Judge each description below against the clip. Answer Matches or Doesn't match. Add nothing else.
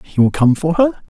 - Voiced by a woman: Doesn't match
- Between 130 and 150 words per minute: Doesn't match